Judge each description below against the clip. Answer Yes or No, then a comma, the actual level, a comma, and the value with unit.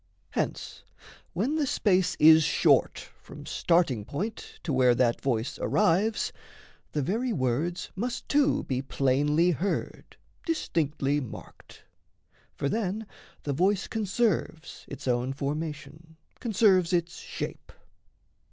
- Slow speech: Yes, slow, 115 wpm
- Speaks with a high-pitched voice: No, medium, 165 Hz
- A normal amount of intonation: No, wide, 6.4 semitones